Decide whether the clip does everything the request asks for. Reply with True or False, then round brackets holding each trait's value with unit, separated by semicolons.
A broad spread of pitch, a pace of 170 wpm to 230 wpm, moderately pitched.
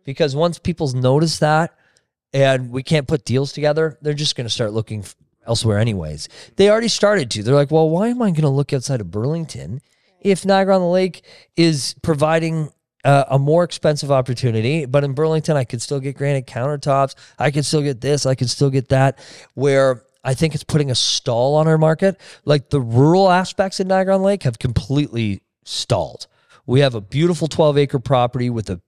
False (3.7 semitones; 200 wpm; 145 Hz)